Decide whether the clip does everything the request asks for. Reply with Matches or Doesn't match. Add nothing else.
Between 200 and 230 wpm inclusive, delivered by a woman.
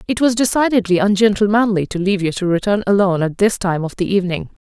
Matches